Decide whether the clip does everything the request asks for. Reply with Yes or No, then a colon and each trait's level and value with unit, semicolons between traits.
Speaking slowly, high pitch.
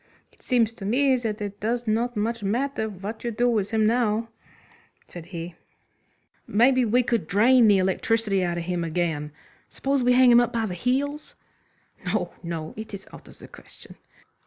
No: average, 180 wpm; high, 220 Hz